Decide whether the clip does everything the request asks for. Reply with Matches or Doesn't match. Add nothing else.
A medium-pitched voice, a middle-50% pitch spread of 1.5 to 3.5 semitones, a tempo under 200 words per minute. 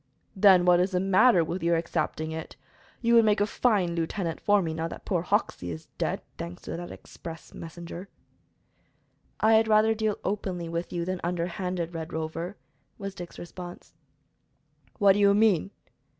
Matches